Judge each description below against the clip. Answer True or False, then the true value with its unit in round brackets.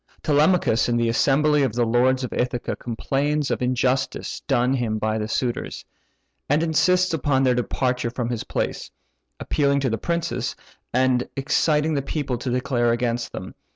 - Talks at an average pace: True (165 wpm)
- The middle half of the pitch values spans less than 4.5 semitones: True (3.3 semitones)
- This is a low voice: True (130 Hz)